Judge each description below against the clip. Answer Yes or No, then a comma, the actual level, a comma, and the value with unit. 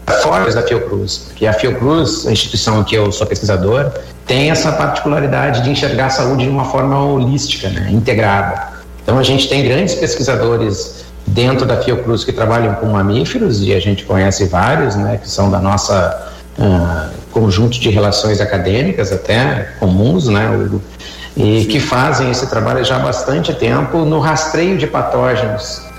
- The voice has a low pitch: Yes, low, 110 Hz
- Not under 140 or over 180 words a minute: Yes, average, 160 wpm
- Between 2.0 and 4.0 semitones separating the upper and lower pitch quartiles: No, average, 4.7 semitones